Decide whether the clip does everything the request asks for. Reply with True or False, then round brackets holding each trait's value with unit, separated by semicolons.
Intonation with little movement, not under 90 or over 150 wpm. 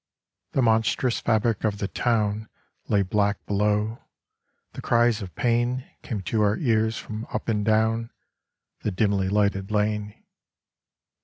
True (1.8 semitones; 135 wpm)